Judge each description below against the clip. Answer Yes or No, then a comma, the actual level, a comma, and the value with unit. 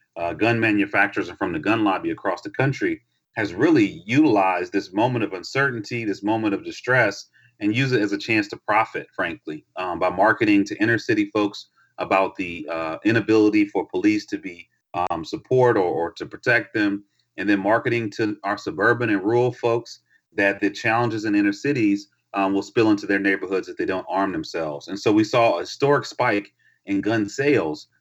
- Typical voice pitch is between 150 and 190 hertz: No, low, 115 Hz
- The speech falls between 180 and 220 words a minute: Yes, average, 190 wpm